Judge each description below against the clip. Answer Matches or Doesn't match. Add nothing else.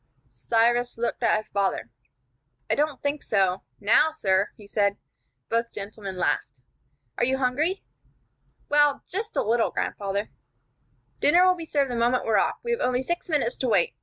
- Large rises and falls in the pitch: Matches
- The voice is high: Matches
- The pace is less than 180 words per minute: Matches